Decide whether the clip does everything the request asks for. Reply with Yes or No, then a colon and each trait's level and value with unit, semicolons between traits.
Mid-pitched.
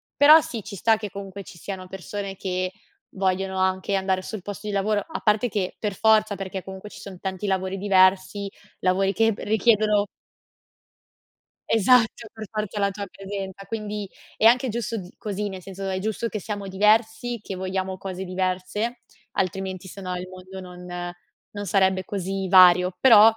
No: high, 195 Hz